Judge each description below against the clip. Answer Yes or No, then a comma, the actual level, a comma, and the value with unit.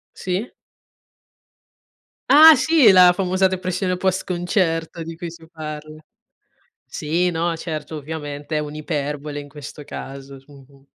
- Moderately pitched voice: Yes, medium, 165 Hz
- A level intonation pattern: No, average, 3.6 semitones